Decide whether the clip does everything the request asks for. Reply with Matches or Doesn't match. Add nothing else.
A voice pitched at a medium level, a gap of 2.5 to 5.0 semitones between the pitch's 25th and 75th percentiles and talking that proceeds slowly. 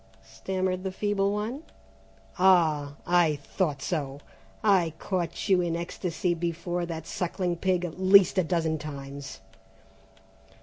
Matches